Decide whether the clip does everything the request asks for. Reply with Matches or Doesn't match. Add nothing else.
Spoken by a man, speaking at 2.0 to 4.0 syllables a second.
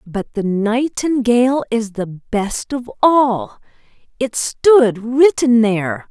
Doesn't match